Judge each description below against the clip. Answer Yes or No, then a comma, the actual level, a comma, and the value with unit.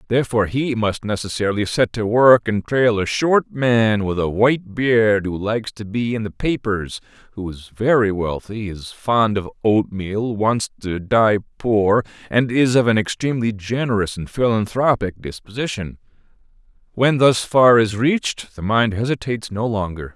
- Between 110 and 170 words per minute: Yes, average, 160 wpm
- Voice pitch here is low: Yes, low, 110 Hz